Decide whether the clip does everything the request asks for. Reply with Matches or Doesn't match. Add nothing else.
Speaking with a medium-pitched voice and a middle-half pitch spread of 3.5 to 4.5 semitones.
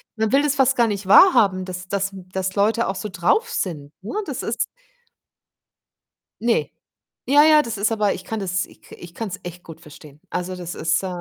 Doesn't match